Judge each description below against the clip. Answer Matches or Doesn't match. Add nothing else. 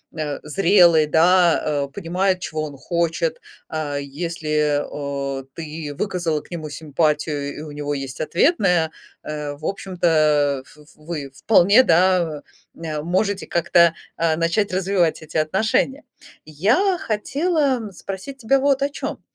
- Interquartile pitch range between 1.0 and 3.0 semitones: Doesn't match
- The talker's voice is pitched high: Doesn't match